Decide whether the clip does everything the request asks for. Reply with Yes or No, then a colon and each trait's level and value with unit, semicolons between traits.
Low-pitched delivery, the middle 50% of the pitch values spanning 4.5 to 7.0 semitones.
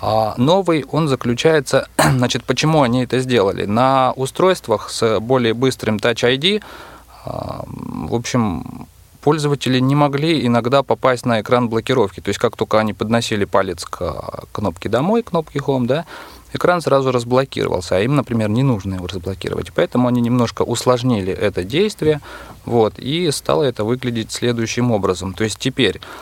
No: low, 125 Hz; average, 3.2 semitones